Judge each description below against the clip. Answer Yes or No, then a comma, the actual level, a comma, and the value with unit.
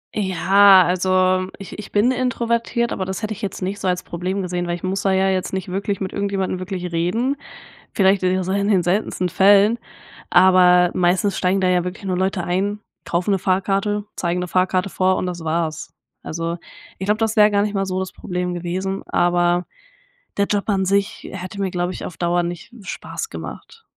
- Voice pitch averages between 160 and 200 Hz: Yes, high, 190 Hz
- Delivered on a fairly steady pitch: Yes, narrow, 2.0 semitones